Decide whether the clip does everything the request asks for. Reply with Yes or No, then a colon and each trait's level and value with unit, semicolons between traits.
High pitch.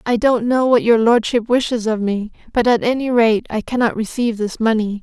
Yes: high, 230 Hz